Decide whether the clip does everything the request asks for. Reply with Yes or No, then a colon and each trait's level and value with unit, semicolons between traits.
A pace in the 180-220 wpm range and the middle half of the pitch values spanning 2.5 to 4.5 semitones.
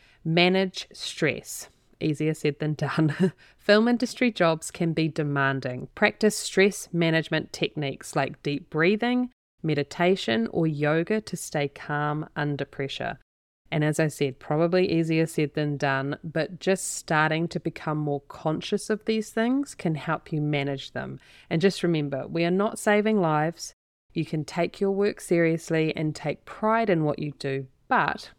No: average, 155 wpm; average, 4.0 semitones